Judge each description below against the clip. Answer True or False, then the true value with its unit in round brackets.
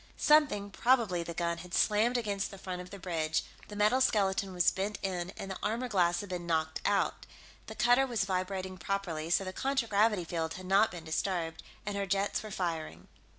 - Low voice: False (190 Hz)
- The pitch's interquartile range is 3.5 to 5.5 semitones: False (3.1 semitones)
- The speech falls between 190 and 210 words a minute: True (195 wpm)